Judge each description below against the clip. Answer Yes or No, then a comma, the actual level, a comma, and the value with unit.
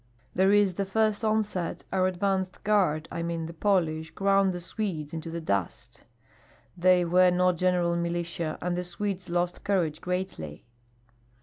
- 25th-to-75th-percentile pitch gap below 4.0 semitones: Yes, narrow, 2.4 semitones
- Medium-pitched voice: Yes, medium, 180 Hz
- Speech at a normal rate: Yes, average, 150 wpm